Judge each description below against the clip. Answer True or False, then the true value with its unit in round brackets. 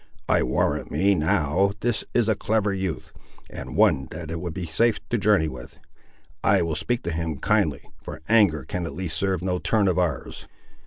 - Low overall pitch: True (90 Hz)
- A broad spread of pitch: False (4.3 semitones)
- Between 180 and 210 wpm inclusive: True (195 wpm)